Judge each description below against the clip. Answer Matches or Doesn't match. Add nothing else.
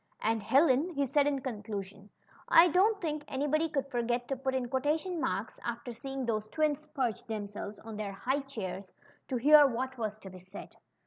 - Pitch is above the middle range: Matches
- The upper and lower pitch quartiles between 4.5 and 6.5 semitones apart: Matches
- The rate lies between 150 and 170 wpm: Doesn't match